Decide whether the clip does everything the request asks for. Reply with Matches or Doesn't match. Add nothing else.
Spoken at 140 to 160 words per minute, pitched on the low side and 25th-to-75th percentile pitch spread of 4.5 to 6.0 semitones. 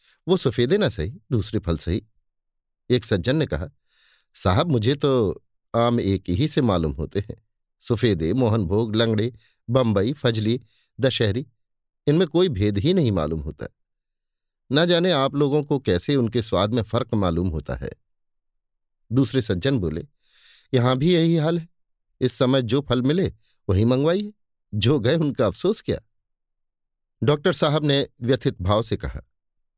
Matches